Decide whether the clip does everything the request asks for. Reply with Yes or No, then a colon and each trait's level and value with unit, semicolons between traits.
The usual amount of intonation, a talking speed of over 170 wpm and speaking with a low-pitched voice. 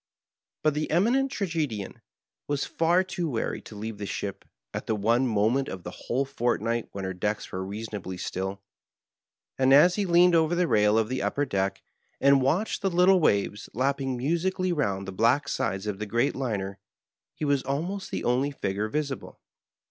No: wide, 7.5 semitones; average, 180 wpm; low, 130 Hz